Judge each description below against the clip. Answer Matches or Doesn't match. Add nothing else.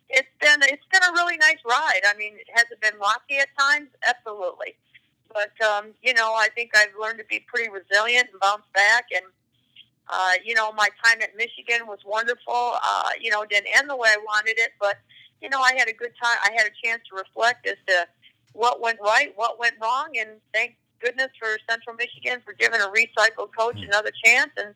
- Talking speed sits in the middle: Doesn't match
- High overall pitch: Matches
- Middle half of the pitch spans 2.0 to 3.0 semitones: Matches